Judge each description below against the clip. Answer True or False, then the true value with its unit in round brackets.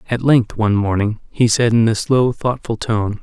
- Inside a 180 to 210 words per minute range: True (205 wpm)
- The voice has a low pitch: True (110 Hz)